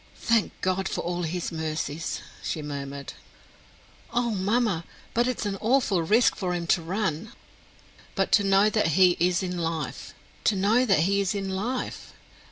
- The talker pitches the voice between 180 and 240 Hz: Yes, high, 190 Hz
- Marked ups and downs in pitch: No, average, 4.3 semitones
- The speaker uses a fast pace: No, average, 170 wpm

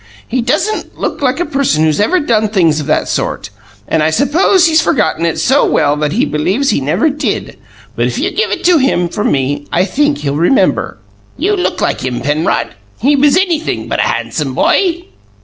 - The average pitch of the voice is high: Yes, very high, 250 Hz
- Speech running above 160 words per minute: Yes, average, 200 wpm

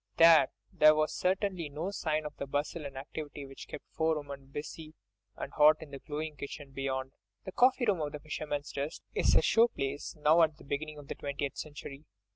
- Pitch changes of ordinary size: No, narrow, 2.0 semitones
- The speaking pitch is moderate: Yes, medium, 150 Hz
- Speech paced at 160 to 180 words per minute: No, fast, 205 wpm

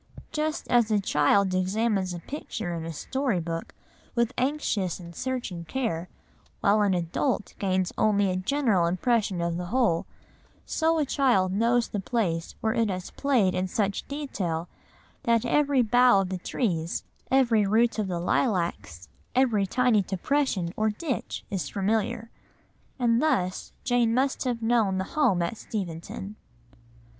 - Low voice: No, high, 210 Hz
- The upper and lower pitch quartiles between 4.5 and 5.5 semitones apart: Yes, average, 5.1 semitones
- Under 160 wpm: Yes, average, 150 wpm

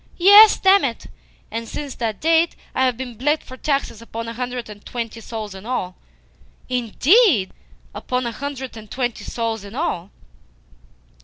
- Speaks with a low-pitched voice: No, high, 245 Hz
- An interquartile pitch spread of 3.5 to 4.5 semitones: Yes, average, 3.9 semitones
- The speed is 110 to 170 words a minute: Yes, average, 160 wpm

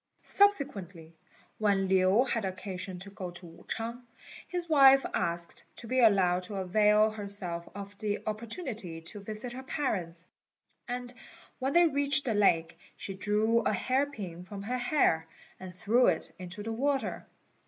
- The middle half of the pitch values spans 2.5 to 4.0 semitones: No, average, 5.1 semitones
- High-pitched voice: Yes, high, 210 Hz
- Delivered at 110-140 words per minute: No, average, 155 wpm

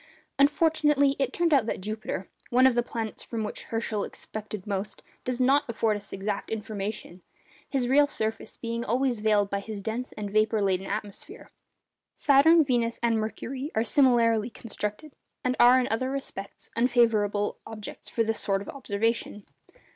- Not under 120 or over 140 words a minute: No, average, 160 wpm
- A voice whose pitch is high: Yes, high, 225 Hz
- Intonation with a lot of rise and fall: No, average, 3.4 semitones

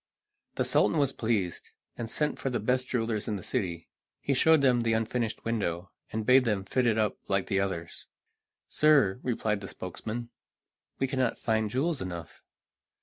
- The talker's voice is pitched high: No, low, 115 Hz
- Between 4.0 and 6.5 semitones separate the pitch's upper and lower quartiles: Yes, average, 4.5 semitones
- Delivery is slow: No, average, 170 wpm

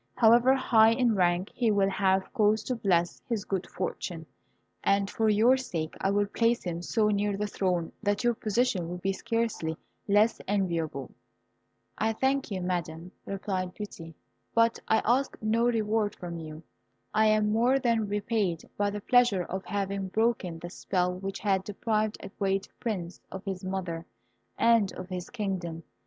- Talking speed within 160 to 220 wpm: Yes, average, 165 wpm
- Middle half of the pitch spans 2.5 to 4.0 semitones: Yes, average, 3.5 semitones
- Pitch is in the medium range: No, high, 200 Hz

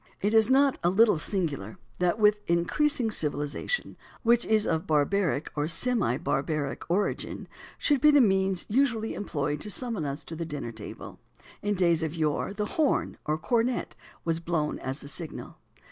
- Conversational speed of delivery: Yes, average, 175 wpm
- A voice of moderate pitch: Yes, medium, 180 Hz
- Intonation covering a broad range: Yes, wide, 6.4 semitones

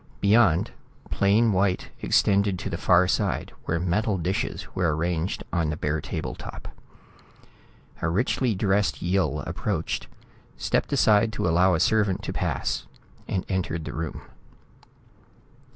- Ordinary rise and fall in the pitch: Yes, average, 3.3 semitones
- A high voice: No, very low, 95 Hz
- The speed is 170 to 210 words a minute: No, slow, 135 wpm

